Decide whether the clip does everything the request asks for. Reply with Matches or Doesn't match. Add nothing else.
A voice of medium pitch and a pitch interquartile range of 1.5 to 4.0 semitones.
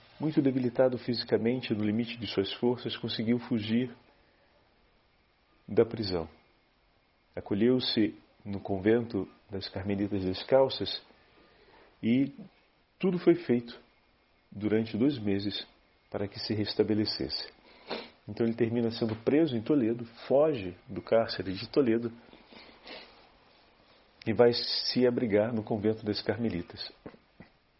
Doesn't match